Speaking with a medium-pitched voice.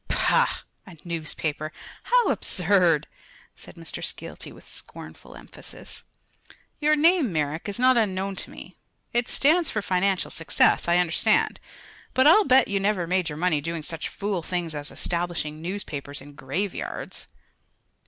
Yes: medium, 180 Hz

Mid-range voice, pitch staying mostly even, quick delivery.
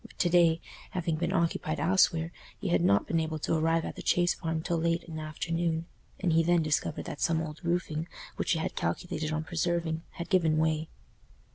Yes: medium, 165 Hz; narrow, 1.4 semitones; fast, 210 wpm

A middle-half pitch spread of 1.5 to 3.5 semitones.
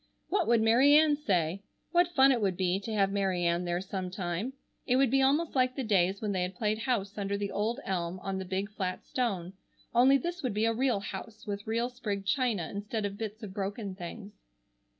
No: average, 4.4 semitones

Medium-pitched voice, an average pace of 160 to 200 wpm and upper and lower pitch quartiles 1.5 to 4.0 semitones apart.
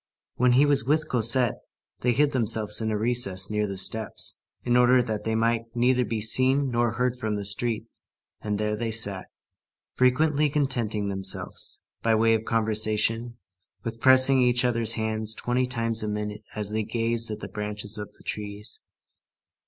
No: low, 115 Hz; average, 170 wpm; narrow, 2.6 semitones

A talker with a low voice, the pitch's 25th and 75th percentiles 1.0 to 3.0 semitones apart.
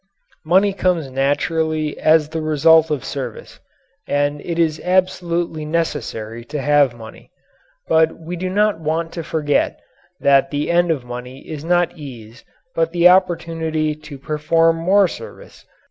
No: medium, 160 Hz; average, 2.7 semitones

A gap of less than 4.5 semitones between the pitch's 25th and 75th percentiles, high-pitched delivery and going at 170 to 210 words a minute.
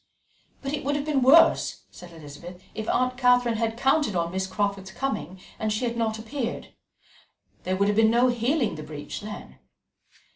No: average, 5.0 semitones; high, 225 Hz; average, 180 wpm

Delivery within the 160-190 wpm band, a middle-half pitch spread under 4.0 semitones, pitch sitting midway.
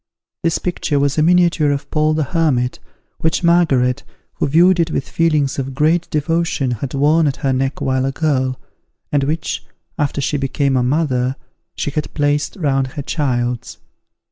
Yes: average, 170 wpm; average, 3.2 semitones; medium, 145 Hz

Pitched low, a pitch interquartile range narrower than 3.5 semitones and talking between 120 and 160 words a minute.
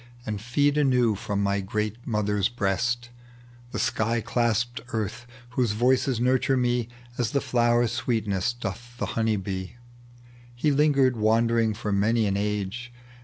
Yes: low, 115 Hz; average, 2.7 semitones; average, 140 wpm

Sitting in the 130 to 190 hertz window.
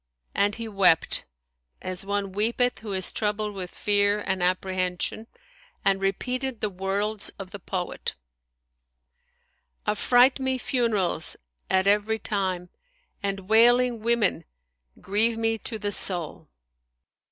No: high, 205 Hz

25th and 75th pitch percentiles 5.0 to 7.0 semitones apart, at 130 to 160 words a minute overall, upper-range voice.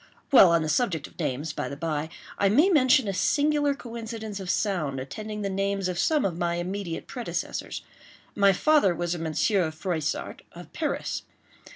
No: wide, 5.5 semitones; average, 175 wpm; high, 195 Hz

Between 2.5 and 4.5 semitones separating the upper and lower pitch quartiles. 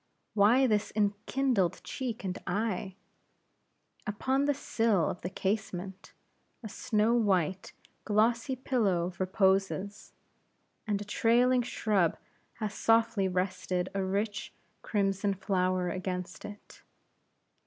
Yes: average, 3.2 semitones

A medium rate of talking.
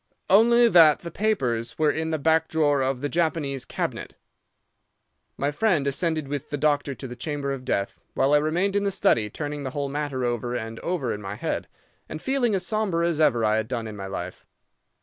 No: fast, 210 wpm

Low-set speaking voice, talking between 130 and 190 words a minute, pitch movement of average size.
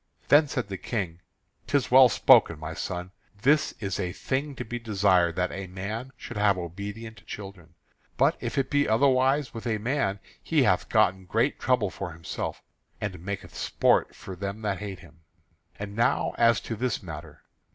Yes: low, 100 Hz; average, 175 wpm; average, 4.9 semitones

